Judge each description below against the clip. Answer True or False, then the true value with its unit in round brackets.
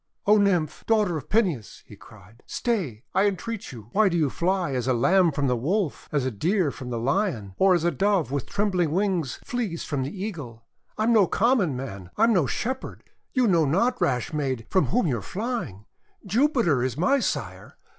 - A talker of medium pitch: True (175 Hz)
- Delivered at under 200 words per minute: False (205 wpm)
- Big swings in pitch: True (7.9 semitones)